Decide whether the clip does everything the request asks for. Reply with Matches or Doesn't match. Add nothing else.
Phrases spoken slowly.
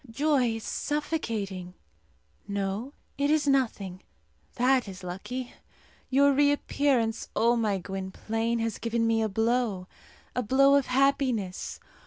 Matches